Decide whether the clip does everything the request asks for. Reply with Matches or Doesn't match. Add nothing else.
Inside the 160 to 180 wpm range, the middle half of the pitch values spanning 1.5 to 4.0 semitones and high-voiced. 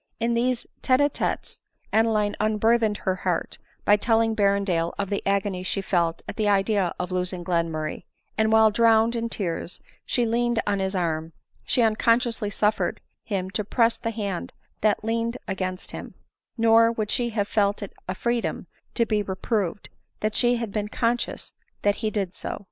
Matches